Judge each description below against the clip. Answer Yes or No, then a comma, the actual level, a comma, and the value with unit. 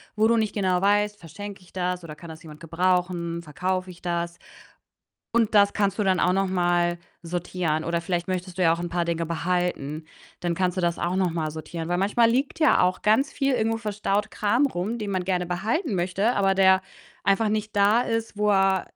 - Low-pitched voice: No, medium, 185 Hz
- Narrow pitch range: No, average, 3.1 semitones